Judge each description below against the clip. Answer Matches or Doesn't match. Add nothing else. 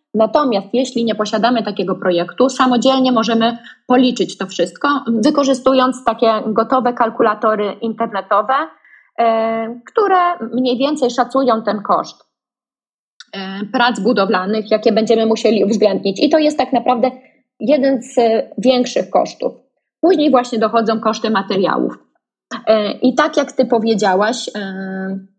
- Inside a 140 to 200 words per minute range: Doesn't match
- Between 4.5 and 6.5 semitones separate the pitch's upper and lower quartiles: Doesn't match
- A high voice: Matches